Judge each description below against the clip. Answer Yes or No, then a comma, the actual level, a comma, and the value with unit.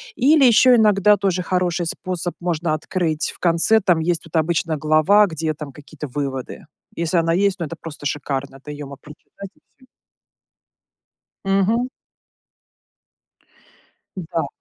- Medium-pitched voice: Yes, medium, 170 Hz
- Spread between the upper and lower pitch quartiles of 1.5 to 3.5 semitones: No, average, 4.1 semitones